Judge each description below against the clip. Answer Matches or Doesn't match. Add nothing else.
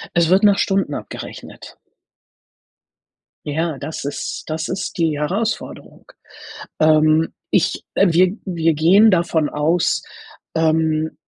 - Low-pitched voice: Doesn't match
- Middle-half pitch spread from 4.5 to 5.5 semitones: Doesn't match